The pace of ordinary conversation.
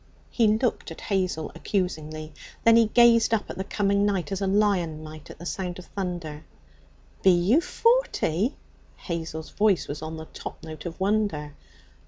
Yes: average, 170 wpm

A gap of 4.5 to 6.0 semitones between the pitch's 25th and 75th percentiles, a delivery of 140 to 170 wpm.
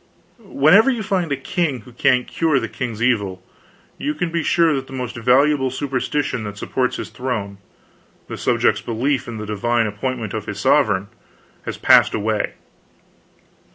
Yes: average, 5.2 semitones; average, 160 wpm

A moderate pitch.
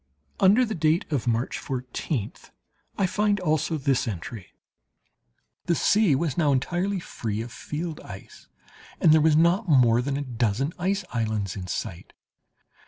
Yes: medium, 145 Hz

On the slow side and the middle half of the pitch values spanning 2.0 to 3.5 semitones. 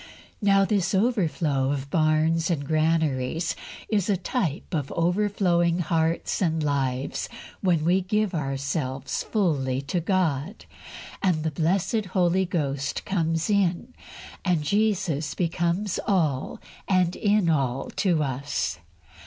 No: slow, 120 wpm; average, 4.4 semitones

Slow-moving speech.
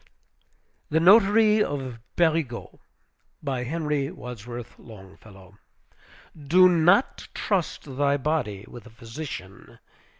Yes: slow, 95 wpm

